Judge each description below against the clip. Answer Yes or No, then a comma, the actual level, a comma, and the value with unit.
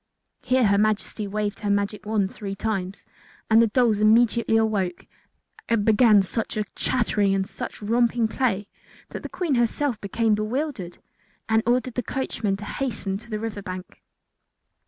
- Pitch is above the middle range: Yes, high, 215 Hz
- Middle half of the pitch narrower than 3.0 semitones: Yes, narrow, 2.6 semitones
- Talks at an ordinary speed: Yes, average, 155 wpm